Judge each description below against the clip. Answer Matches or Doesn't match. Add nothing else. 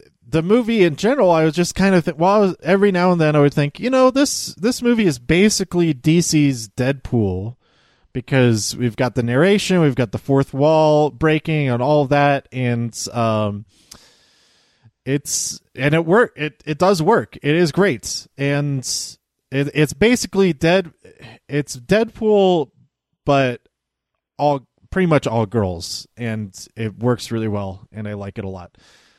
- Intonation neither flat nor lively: Doesn't match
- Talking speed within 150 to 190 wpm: Matches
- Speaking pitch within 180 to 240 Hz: Doesn't match